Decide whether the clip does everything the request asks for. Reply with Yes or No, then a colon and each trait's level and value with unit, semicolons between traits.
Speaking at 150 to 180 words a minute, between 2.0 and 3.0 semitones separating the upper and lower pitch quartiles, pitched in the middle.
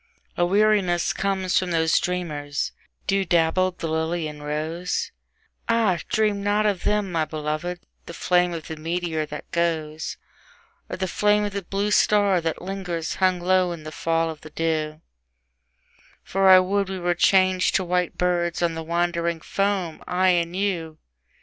Yes: average, 165 wpm; average, 2.7 semitones; medium, 175 Hz